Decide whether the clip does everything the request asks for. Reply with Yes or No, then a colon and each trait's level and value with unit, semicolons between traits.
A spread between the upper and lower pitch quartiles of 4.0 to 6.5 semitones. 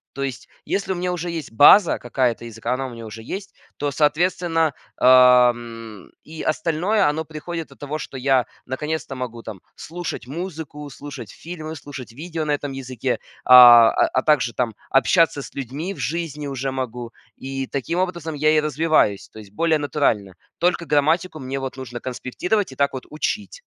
Yes: average, 4.3 semitones